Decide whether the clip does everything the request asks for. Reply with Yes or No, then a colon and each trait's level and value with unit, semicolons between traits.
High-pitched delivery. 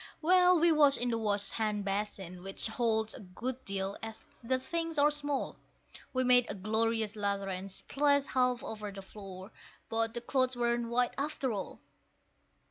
Yes: high, 230 Hz